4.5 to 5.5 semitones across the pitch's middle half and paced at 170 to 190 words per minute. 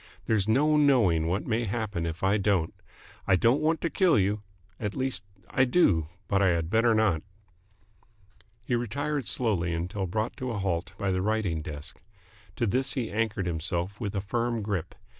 Yes: average, 4.8 semitones; average, 180 wpm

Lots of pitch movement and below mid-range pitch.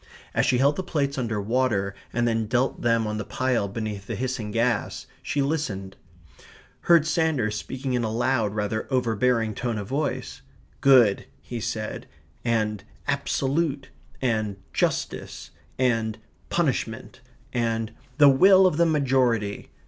No: average, 3.9 semitones; low, 120 Hz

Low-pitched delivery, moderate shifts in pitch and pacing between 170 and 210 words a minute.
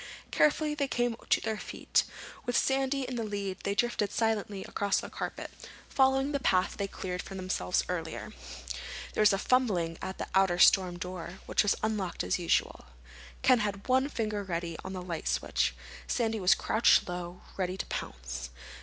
No: high, 200 Hz; average, 4.8 semitones; average, 180 wpm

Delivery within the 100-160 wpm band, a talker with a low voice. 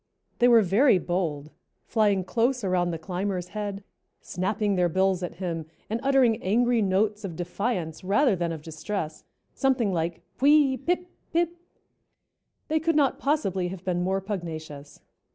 No: average, 150 wpm; high, 195 Hz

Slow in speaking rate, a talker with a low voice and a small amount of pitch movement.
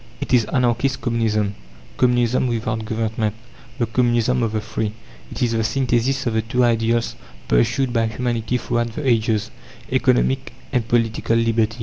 No: average, 150 wpm; low, 115 Hz; narrow, 1.6 semitones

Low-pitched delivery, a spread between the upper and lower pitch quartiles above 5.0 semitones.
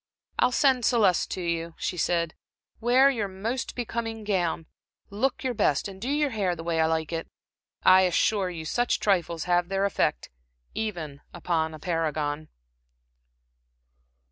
No: medium, 185 Hz; wide, 5.4 semitones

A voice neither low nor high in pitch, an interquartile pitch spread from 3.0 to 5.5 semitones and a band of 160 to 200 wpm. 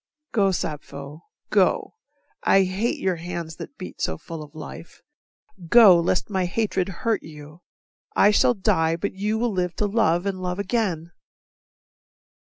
No: medium, 180 Hz; average, 3.7 semitones; average, 150 wpm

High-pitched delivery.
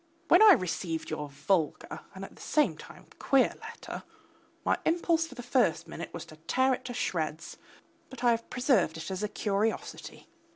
Yes: high, 215 Hz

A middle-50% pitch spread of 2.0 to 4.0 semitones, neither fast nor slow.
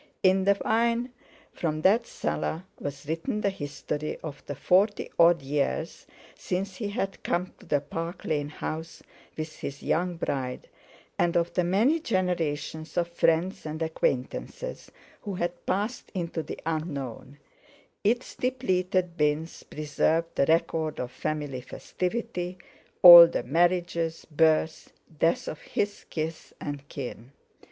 No: average, 3.5 semitones; slow, 130 wpm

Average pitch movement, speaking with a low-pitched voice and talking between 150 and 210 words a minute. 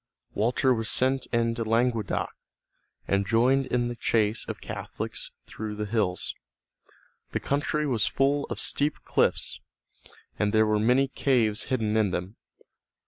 No: average, 3.3 semitones; low, 115 Hz; average, 140 wpm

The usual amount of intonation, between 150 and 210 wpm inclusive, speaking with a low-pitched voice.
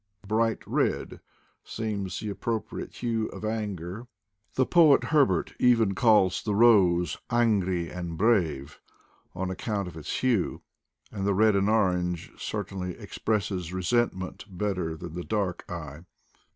No: average, 3.7 semitones; average, 140 wpm; low, 100 Hz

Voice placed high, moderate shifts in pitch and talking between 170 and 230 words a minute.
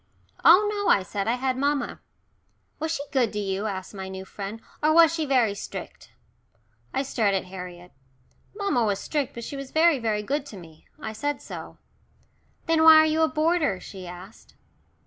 No: high, 245 Hz; wide, 7.9 semitones; average, 185 wpm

